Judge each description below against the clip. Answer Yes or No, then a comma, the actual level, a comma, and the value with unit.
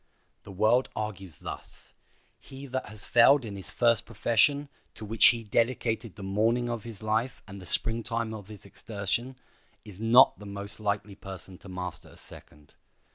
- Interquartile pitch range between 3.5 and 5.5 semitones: No, average, 2.8 semitones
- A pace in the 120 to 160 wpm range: No, average, 175 wpm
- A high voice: No, low, 110 Hz